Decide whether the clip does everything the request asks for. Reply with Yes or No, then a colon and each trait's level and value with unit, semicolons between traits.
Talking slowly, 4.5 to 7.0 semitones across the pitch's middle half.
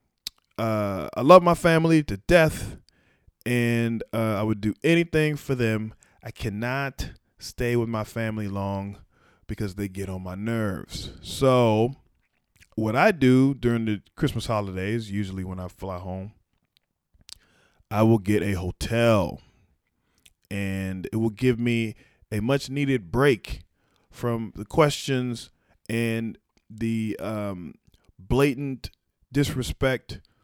No: slow, 125 wpm; average, 3.9 semitones